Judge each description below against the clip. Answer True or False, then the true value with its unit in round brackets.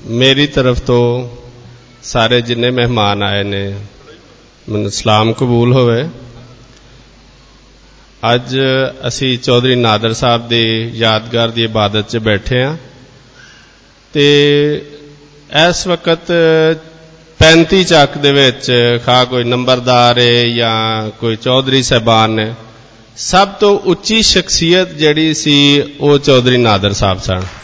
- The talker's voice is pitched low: True (125 Hz)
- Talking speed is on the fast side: False (110 wpm)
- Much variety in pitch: False (4.1 semitones)